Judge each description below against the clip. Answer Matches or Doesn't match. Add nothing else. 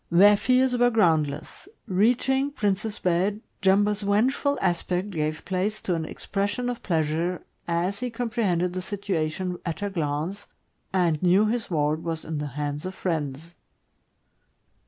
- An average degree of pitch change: Matches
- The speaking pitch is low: Doesn't match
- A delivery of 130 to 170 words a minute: Matches